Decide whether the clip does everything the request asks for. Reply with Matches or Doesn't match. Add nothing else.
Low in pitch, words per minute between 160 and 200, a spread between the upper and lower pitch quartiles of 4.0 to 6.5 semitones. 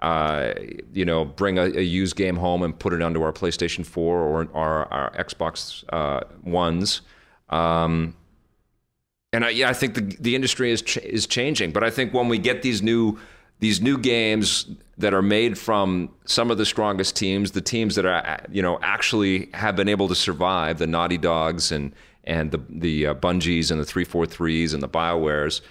Matches